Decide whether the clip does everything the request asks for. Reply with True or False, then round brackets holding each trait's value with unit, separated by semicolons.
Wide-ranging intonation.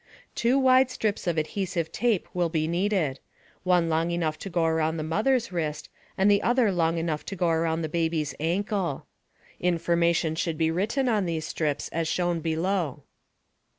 False (3.3 semitones)